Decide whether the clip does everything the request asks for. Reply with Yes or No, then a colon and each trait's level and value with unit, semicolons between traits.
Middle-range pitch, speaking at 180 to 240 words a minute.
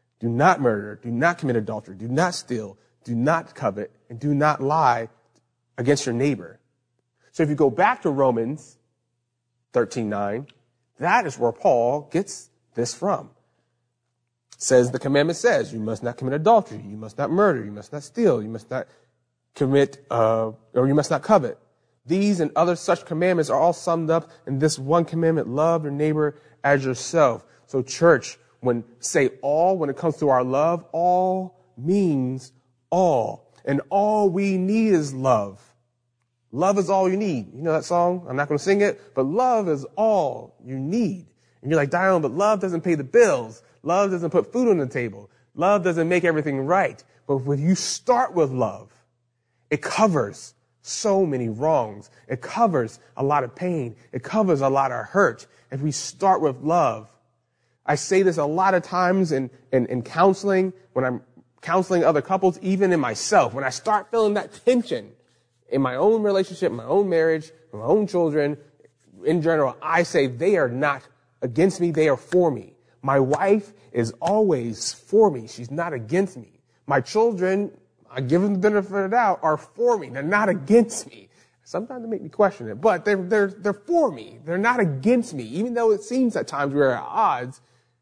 Yes: medium, 150 Hz; average, 185 wpm